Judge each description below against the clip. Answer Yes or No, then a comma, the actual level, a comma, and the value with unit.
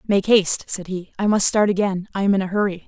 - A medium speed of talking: No, fast, 270 wpm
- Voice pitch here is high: Yes, high, 195 Hz